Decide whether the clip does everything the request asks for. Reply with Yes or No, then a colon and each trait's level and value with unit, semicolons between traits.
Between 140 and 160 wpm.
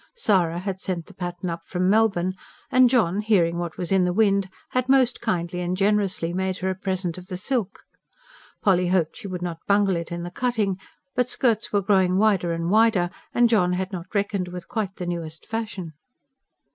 No: average, 195 wpm